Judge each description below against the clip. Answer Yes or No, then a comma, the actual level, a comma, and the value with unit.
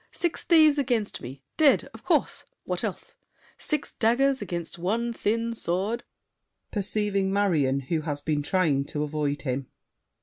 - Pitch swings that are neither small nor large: No, wide, 7.8 semitones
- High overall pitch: Yes, high, 195 Hz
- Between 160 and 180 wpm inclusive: No, average, 140 wpm